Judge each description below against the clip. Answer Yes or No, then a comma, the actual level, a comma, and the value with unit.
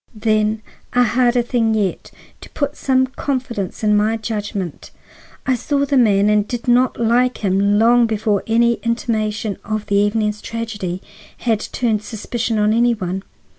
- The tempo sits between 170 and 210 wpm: No, average, 150 wpm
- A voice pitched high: Yes, high, 220 Hz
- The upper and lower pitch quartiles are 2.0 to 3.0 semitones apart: Yes, narrow, 2.4 semitones